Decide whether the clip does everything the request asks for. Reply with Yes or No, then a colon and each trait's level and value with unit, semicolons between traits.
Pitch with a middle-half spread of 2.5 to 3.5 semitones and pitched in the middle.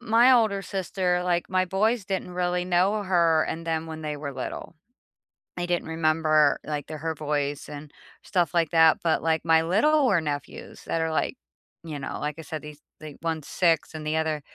Yes: average, 2.8 semitones; medium, 165 Hz